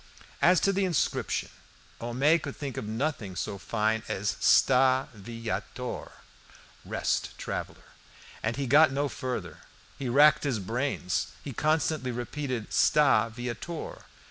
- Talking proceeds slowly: Yes, slow, 115 wpm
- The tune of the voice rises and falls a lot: No, average, 4.3 semitones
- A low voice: Yes, low, 130 Hz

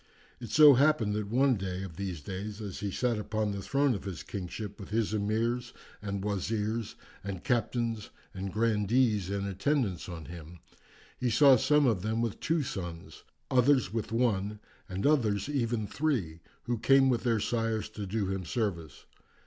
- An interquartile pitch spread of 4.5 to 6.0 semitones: No, average, 3.8 semitones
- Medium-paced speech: Yes, average, 170 wpm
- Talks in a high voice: No, low, 105 Hz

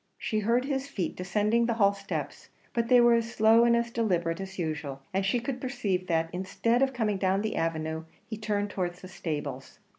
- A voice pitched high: Yes, high, 205 Hz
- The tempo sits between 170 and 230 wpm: Yes, fast, 205 wpm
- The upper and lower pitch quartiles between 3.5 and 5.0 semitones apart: Yes, average, 4.6 semitones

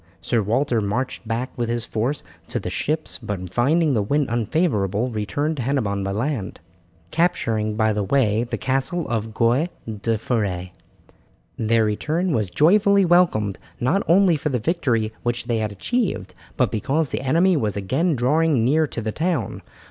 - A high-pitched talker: No, low, 120 Hz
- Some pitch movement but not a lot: No, wide, 6.1 semitones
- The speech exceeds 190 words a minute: No, average, 165 wpm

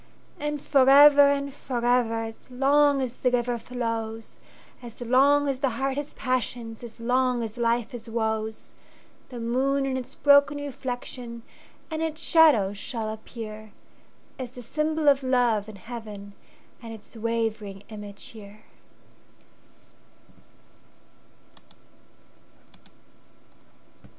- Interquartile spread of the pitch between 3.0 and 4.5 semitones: Yes, average, 3.4 semitones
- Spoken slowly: Yes, slow, 95 wpm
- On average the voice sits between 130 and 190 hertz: No, high, 245 Hz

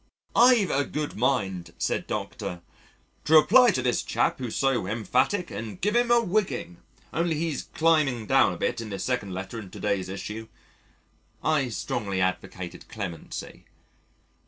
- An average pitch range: No, wide, 8.2 semitones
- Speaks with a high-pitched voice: No, low, 120 Hz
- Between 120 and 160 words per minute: Yes, average, 155 wpm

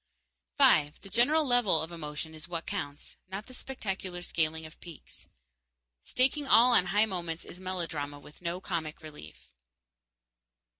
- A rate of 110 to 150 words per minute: Yes, average, 145 wpm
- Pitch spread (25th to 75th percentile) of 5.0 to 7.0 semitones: Yes, average, 5.3 semitones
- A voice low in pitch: No, medium, 175 Hz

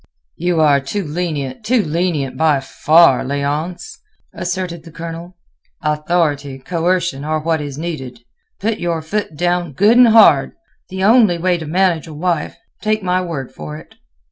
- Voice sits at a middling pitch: Yes, medium, 165 Hz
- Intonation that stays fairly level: No, average, 3.5 semitones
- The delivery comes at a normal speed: Yes, average, 155 wpm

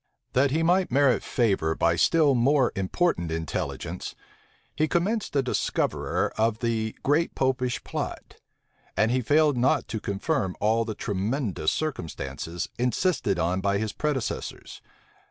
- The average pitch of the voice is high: No, low, 120 Hz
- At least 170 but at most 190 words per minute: No, slow, 135 wpm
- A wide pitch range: Yes, wide, 6.7 semitones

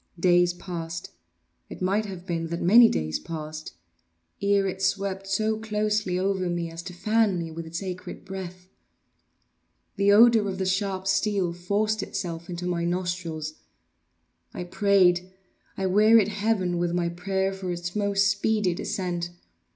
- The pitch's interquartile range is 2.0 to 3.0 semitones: Yes, narrow, 2.6 semitones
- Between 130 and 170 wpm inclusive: Yes, average, 140 wpm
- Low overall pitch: No, medium, 185 Hz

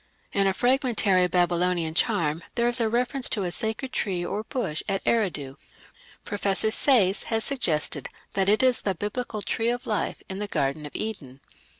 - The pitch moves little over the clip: No, average, 5.0 semitones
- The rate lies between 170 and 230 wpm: Yes, average, 175 wpm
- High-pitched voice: Yes, high, 200 Hz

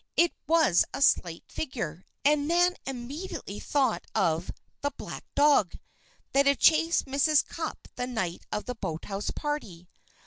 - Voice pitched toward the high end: Yes, very high, 275 Hz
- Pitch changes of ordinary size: No, wide, 8.0 semitones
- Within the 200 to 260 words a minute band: No, average, 140 wpm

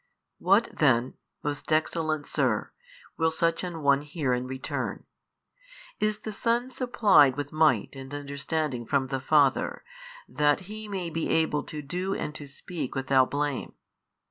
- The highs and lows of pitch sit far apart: No, average, 3.6 semitones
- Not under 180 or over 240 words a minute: No, average, 150 wpm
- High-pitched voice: No, medium, 150 Hz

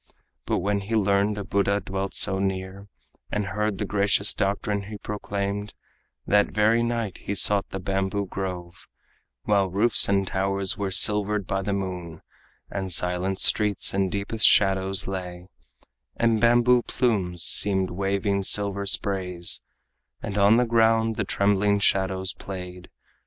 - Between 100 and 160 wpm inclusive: Yes, average, 140 wpm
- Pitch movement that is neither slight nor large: No, narrow, 1.5 semitones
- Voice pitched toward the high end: No, low, 100 Hz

